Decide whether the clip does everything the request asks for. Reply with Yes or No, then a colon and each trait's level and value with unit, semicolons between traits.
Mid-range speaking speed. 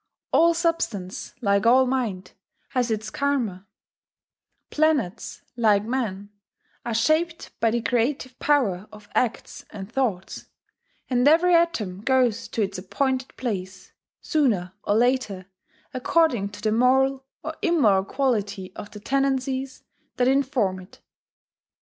No: slow, 125 wpm